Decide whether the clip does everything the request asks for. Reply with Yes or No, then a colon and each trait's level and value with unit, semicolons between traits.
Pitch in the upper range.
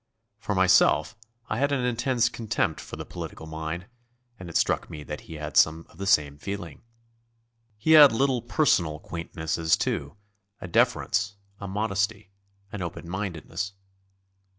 No: very low, 95 Hz